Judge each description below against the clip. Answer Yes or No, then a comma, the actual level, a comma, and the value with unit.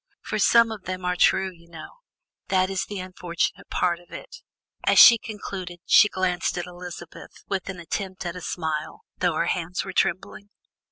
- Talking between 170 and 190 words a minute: Yes, average, 180 wpm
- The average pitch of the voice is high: No, medium, 180 Hz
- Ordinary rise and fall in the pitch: No, narrow, 1.6 semitones